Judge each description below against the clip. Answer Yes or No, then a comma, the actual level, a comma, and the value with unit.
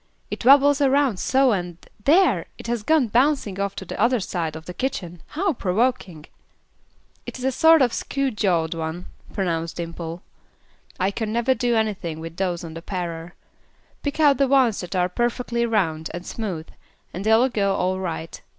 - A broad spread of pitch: Yes, wide, 6.8 semitones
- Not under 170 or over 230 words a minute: Yes, average, 180 wpm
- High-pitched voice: Yes, high, 205 Hz